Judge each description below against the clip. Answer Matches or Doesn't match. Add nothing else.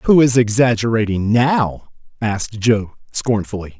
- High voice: Doesn't match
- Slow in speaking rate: Matches